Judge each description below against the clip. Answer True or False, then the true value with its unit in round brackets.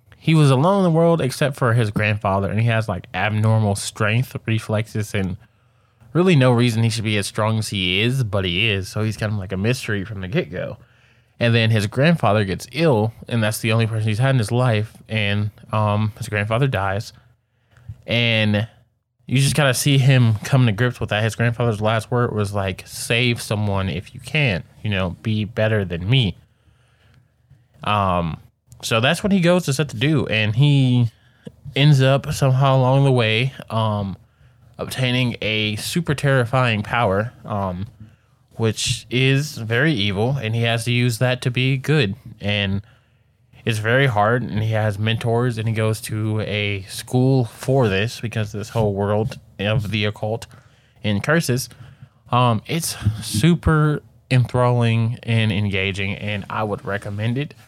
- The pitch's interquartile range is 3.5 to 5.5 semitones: False (3.1 semitones)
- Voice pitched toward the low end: True (115 Hz)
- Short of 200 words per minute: True (175 wpm)